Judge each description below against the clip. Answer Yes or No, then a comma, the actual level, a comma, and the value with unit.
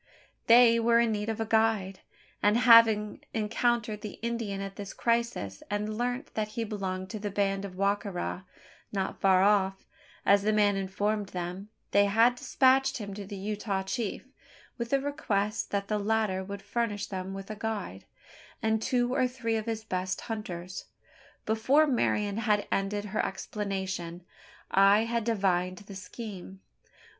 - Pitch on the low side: No, high, 210 Hz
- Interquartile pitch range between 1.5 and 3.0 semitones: Yes, narrow, 2.6 semitones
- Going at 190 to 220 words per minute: No, average, 165 wpm